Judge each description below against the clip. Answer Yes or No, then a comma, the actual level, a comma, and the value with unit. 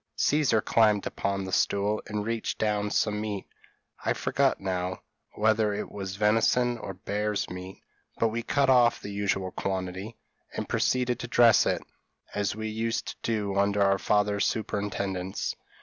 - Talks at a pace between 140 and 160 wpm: Yes, average, 155 wpm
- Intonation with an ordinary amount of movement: No, narrow, 2.2 semitones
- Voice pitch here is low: Yes, low, 105 Hz